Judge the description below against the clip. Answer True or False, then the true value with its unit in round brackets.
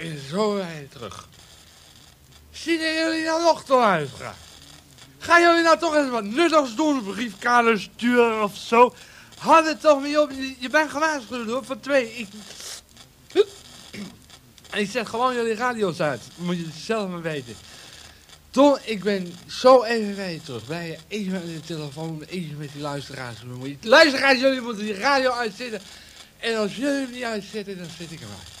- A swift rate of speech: False (170 wpm)